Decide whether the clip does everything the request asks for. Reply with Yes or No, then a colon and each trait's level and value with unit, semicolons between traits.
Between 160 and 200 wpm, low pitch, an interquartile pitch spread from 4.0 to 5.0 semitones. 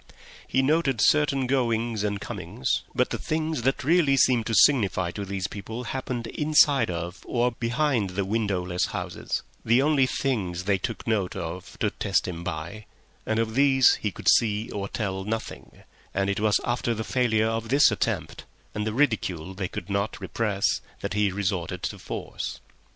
Yes: average, 165 wpm; low, 110 Hz; average, 4.7 semitones